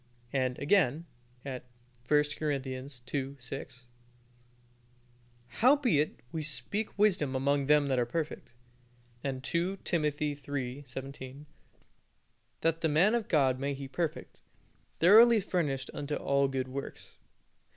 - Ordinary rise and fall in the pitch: Yes, average, 3.6 semitones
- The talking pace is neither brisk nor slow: No, slow, 120 wpm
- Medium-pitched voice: Yes, medium, 145 Hz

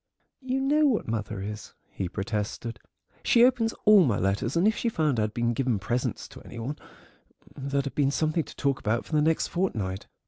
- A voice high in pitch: No, low, 135 Hz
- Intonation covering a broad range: Yes, wide, 8.6 semitones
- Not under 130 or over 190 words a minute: No, average, 200 wpm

